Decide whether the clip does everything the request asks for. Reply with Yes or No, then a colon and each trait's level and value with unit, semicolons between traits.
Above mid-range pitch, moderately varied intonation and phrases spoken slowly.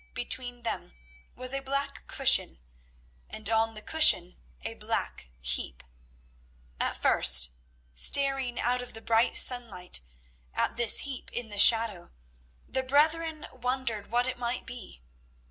Yes: high, 245 Hz; average, 3.3 semitones; slow, 130 wpm